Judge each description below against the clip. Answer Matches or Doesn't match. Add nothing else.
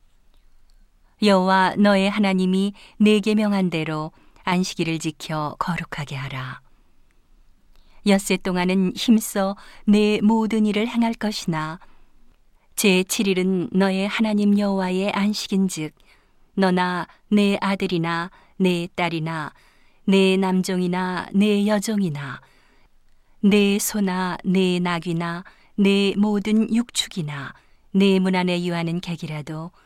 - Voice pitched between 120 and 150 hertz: Doesn't match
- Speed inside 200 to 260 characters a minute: Matches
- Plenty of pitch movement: Doesn't match